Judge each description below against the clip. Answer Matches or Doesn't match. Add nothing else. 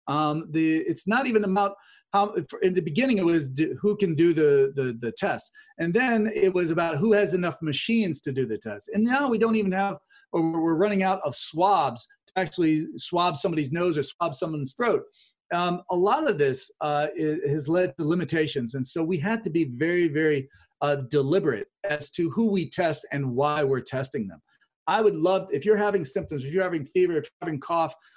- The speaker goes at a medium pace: Doesn't match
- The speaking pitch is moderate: Matches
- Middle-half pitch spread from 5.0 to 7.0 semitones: Doesn't match